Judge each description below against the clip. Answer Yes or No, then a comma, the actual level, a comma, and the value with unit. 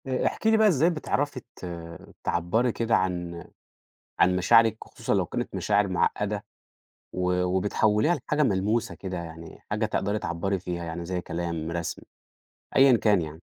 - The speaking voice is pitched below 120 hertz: Yes, low, 100 Hz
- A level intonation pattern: No, average, 5.0 semitones